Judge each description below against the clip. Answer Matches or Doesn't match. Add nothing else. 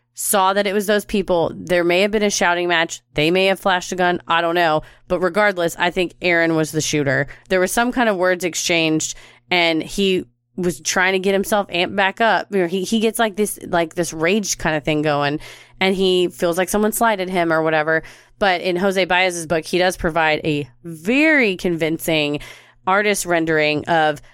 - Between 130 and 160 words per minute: Doesn't match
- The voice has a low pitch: Doesn't match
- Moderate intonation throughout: Matches